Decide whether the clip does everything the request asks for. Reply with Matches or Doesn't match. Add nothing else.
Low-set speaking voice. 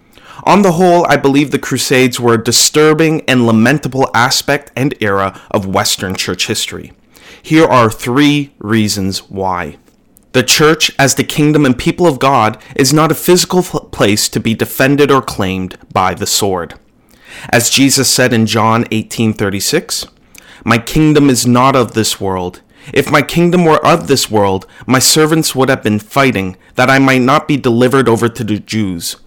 Matches